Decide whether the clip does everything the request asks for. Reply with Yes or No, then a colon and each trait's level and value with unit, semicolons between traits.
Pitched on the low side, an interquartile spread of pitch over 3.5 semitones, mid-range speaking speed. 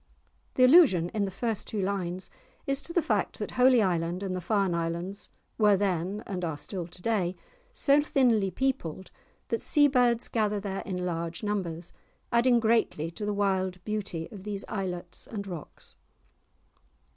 No: high, 195 Hz; average, 4.2 semitones; average, 170 wpm